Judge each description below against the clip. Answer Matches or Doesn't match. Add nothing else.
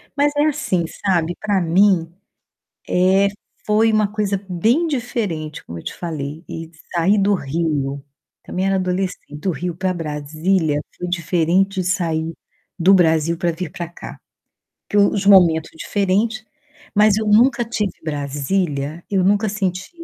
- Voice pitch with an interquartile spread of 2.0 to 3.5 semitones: Doesn't match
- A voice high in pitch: Doesn't match